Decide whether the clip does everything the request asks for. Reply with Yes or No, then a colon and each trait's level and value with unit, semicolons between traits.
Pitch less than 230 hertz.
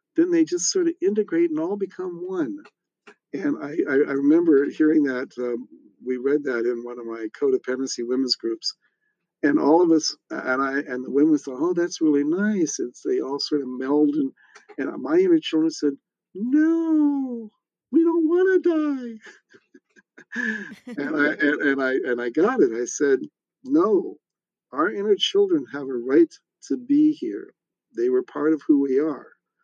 No: very high, 270 Hz